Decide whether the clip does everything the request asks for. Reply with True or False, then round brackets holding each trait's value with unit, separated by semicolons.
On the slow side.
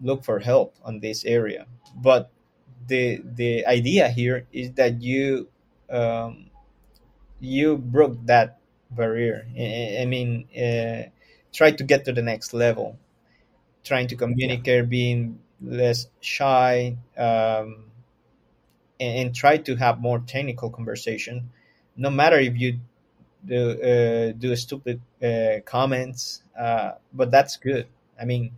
True (130 wpm)